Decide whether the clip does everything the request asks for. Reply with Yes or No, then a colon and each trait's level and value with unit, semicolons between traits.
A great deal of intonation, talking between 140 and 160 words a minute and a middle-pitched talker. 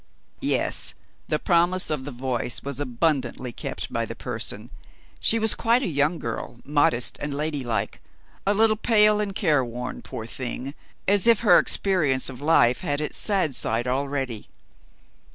Yes: wide, 6.7 semitones; average, 150 wpm; medium, 145 Hz